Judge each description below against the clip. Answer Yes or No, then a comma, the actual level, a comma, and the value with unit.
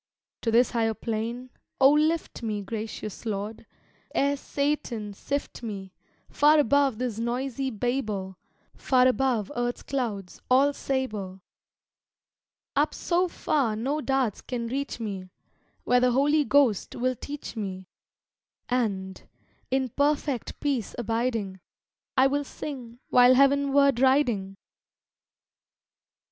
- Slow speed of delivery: Yes, slow, 115 wpm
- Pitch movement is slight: No, average, 4.1 semitones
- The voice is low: No, very high, 250 Hz